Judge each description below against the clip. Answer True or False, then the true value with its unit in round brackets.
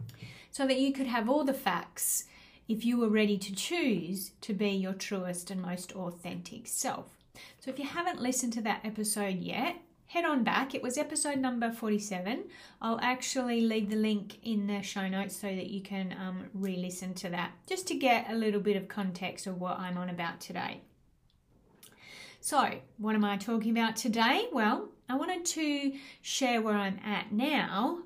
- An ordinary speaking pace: True (185 wpm)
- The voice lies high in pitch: True (215 Hz)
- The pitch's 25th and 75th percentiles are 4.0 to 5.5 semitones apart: True (5.0 semitones)